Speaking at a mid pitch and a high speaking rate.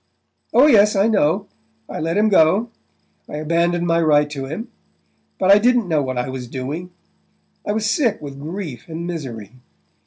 No: medium, 170 Hz; average, 160 wpm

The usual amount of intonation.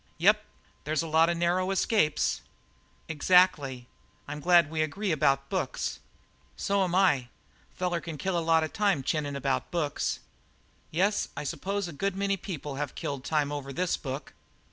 Yes: average, 4.3 semitones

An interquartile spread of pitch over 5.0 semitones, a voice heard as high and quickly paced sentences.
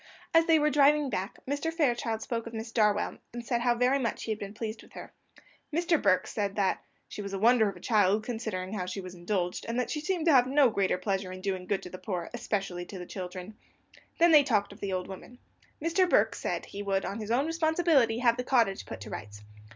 Yes: wide, 5.4 semitones; high, 220 Hz; fast, 245 wpm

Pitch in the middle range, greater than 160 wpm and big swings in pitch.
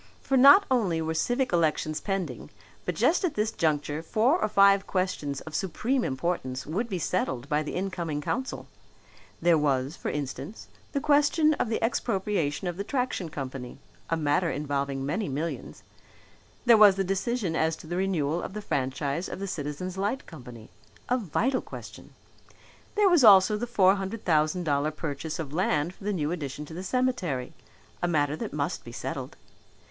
Yes: medium, 175 Hz; average, 175 wpm; wide, 6.1 semitones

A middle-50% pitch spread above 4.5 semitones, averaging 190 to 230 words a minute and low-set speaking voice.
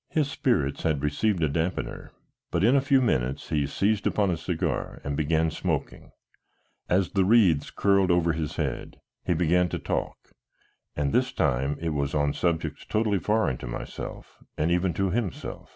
No: average, 5.1 semitones; average, 170 wpm; very low, 85 Hz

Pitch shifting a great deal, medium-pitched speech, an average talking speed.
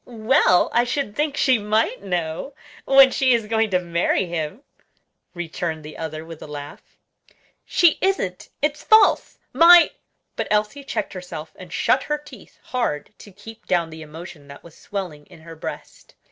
No: wide, 8.1 semitones; high, 195 Hz; average, 165 wpm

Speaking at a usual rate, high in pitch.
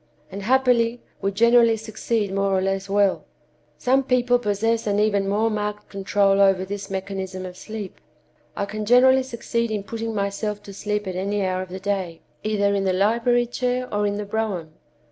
Yes: average, 185 wpm; high, 205 Hz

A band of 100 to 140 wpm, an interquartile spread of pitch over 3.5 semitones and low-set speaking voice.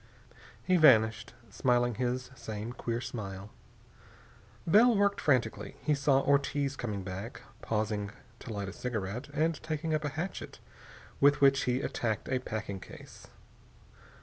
Yes: slow, 135 wpm; average, 4.8 semitones; low, 125 Hz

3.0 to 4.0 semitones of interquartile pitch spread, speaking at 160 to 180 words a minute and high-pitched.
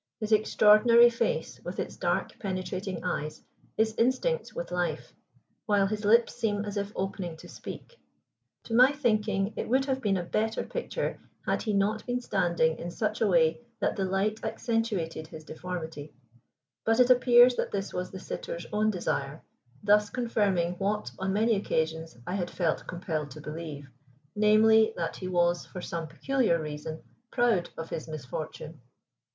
No: average, 4.7 semitones; average, 165 wpm; high, 200 Hz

